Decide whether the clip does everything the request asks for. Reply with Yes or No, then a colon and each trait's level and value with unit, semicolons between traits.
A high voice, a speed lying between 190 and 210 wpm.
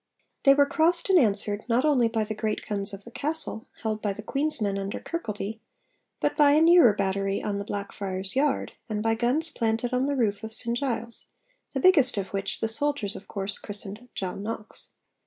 Yes: high, 225 Hz; average, 200 wpm